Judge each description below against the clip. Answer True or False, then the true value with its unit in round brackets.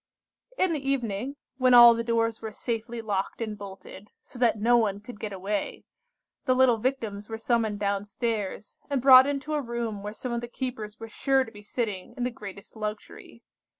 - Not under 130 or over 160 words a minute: False (195 wpm)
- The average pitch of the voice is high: True (230 Hz)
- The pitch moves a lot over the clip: False (3.1 semitones)